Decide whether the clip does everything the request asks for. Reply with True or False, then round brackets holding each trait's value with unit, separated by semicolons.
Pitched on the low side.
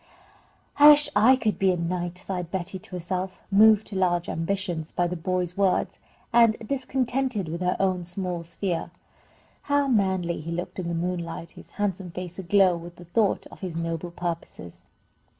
False (180 Hz)